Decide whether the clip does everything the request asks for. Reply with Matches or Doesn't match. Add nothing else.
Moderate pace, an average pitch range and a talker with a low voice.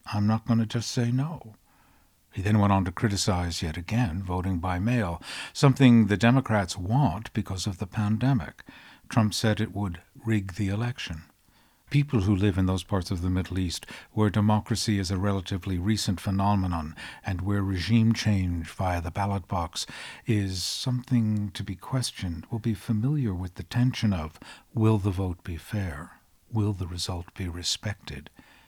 Matches